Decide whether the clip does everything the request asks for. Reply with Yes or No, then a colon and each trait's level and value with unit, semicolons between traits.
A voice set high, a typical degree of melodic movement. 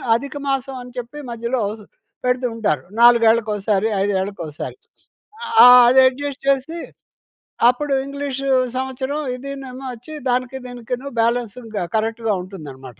Yes: high, 245 Hz; average, 3.2 semitones